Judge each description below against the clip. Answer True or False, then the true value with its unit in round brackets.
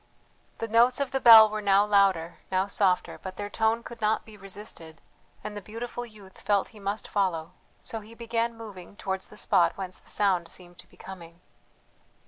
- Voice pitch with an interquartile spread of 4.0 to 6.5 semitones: False (3.0 semitones)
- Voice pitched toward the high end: True (205 Hz)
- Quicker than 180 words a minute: True (190 wpm)